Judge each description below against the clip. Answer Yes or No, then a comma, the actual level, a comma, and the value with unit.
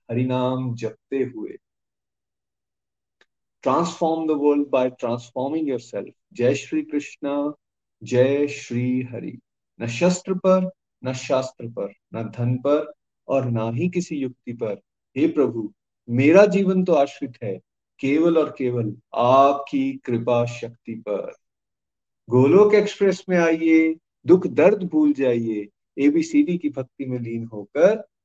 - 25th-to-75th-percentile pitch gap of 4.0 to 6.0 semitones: Yes, average, 5.1 semitones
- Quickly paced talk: No, average, 125 wpm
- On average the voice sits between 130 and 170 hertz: Yes, low, 135 Hz